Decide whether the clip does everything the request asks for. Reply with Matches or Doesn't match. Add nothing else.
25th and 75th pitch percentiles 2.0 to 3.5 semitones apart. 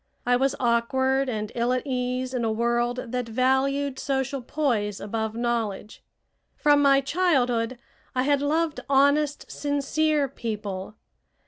Matches